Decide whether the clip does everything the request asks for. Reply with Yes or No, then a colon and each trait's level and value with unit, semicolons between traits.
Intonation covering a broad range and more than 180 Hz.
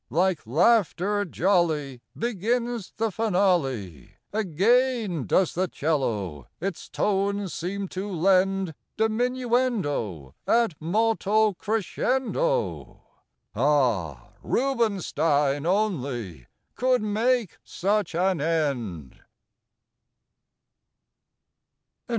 Yes: wide, 7.1 semitones; high, 190 Hz